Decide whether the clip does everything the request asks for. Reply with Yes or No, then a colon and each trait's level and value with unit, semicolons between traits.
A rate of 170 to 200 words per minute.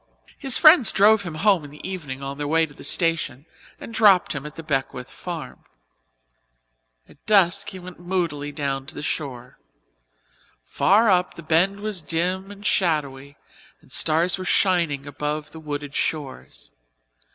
No: average, 160 wpm